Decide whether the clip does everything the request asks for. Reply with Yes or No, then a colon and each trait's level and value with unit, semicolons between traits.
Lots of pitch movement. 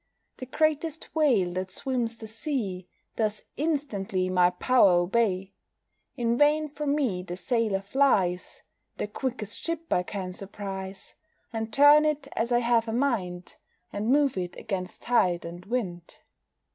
Yes: wide, 6.4 semitones